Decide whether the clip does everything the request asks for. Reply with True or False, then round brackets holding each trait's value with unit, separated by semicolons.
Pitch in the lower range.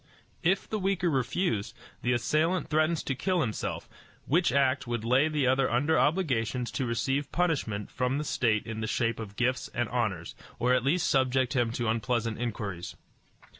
True (125 Hz)